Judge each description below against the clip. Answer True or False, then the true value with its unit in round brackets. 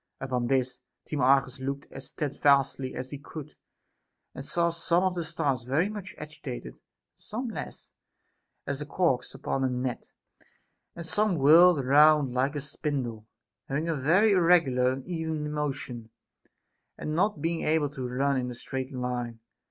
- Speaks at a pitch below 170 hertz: True (140 Hz)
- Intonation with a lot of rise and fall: False (3.9 semitones)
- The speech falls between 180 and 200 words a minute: False (160 wpm)